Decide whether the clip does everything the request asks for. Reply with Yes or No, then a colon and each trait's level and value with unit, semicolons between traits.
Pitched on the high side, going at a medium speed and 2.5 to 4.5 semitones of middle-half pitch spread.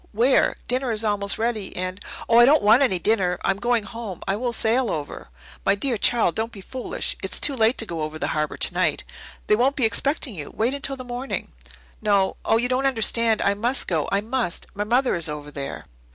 No: high, 220 Hz; fast, 220 wpm; average, 4.1 semitones